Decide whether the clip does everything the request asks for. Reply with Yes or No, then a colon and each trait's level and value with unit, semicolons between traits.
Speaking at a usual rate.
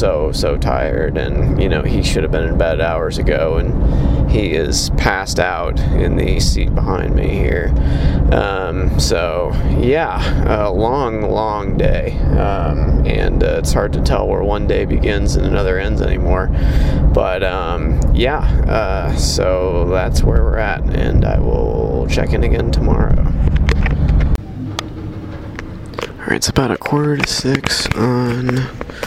Yes: average, 150 wpm